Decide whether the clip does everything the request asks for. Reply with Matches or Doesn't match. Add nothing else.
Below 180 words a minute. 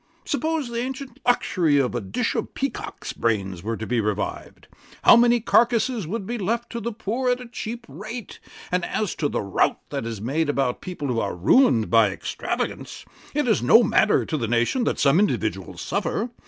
Doesn't match